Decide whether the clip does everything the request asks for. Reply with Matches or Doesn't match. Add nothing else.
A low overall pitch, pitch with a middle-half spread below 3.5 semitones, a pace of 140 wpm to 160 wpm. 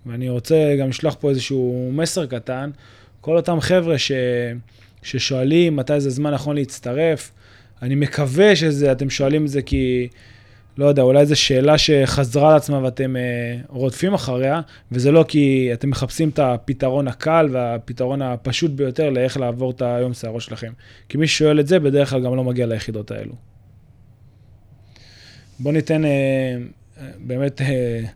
Matches